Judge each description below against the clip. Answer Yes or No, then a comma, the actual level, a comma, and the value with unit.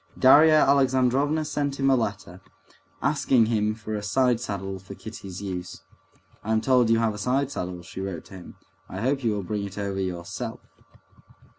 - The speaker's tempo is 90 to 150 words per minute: No, average, 175 wpm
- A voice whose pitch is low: Yes, low, 110 Hz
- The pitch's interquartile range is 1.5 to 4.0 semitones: No, average, 5.2 semitones